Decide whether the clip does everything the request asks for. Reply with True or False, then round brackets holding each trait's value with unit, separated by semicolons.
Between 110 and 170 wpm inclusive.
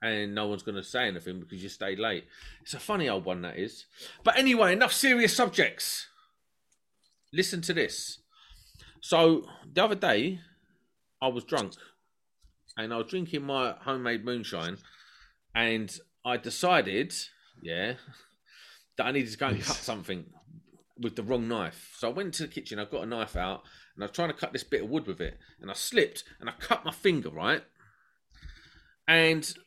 False (180 wpm)